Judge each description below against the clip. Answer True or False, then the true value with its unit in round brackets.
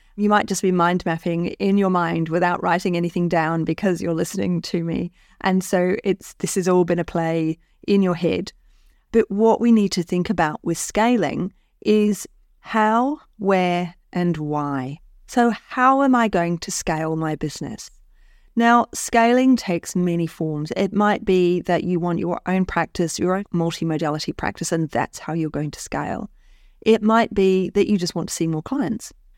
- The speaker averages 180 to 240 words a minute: True (185 wpm)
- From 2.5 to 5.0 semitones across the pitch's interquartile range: True (3.2 semitones)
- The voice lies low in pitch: False (180 Hz)